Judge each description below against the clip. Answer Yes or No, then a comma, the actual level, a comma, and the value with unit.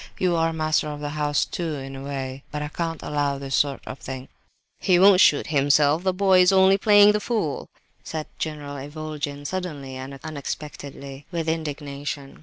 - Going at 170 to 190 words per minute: Yes, average, 180 wpm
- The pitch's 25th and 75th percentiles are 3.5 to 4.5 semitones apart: No, average, 3.1 semitones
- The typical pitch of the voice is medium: Yes, medium, 150 Hz